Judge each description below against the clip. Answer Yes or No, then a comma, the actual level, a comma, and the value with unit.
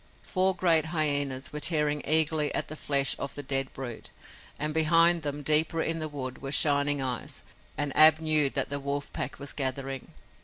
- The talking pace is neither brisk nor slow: Yes, average, 185 wpm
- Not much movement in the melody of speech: Yes, narrow, 2.2 semitones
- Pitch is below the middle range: No, medium, 145 Hz